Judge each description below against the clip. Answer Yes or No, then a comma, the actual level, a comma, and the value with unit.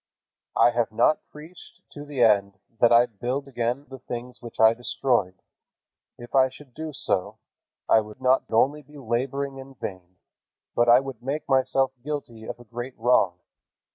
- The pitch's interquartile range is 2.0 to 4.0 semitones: Yes, average, 2.8 semitones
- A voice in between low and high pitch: No, low, 125 Hz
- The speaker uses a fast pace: No, average, 170 wpm